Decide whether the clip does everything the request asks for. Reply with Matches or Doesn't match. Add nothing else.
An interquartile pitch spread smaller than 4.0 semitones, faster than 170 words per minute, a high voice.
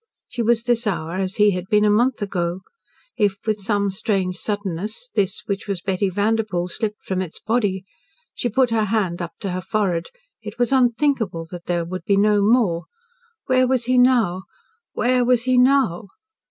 Doesn't match